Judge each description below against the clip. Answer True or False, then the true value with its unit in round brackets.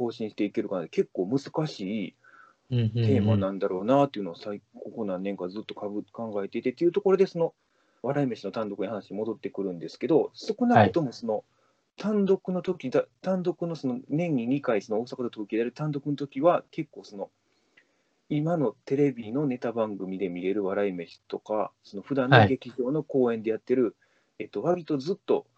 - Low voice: True (130 Hz)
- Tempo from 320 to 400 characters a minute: True (335 characters per minute)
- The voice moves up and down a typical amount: False (7.8 semitones)